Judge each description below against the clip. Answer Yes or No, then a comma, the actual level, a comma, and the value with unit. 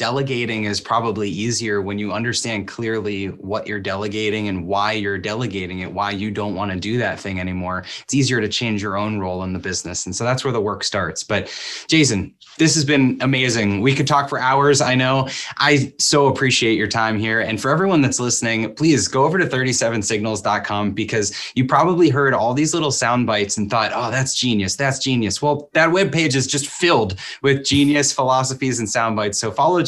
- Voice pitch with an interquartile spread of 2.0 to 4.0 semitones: No, average, 4.8 semitones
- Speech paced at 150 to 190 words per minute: No, fast, 205 wpm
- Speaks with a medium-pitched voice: No, low, 115 Hz